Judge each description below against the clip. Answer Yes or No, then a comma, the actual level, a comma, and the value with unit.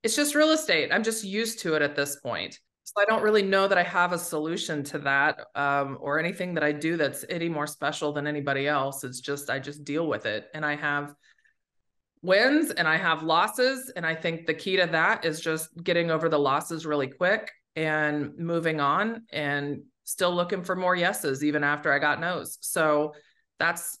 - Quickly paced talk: Yes, fast, 210 wpm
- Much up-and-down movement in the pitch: No, average, 3.5 semitones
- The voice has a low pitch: No, medium, 160 Hz